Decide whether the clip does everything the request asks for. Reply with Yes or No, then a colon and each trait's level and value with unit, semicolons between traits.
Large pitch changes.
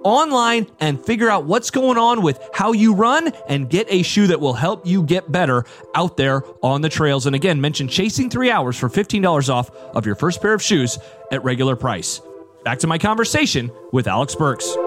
Yes: wide, 7.5 semitones